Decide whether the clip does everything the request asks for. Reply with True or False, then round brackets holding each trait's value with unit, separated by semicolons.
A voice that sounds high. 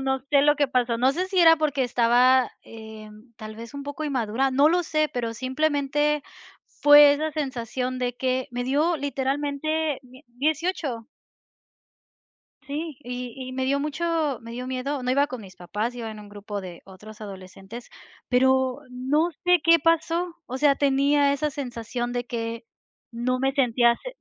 True (260 Hz)